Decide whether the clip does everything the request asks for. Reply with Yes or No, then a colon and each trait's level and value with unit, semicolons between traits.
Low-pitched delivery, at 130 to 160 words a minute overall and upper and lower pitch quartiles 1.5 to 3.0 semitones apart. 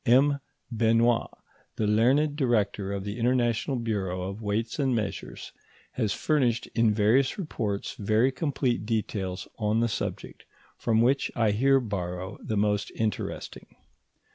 No: low, 115 Hz; slow, 135 wpm; average, 3.4 semitones